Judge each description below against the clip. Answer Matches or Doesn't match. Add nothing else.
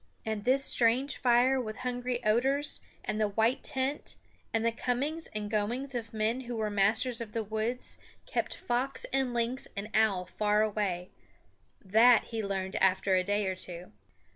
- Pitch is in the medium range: Doesn't match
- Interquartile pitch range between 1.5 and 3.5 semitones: Matches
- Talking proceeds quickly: Doesn't match